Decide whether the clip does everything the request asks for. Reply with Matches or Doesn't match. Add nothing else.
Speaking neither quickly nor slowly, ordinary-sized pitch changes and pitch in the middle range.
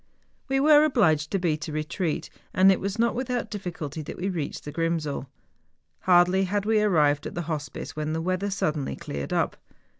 Matches